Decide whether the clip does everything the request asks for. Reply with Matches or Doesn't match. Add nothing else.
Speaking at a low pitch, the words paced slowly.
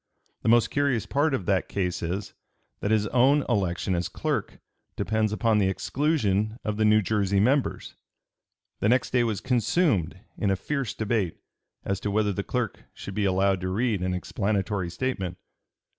Doesn't match